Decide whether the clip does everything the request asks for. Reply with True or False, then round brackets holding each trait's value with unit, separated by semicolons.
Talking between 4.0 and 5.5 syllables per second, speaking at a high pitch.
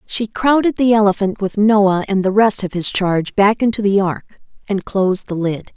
True (4.9 syllables/s; 205 Hz)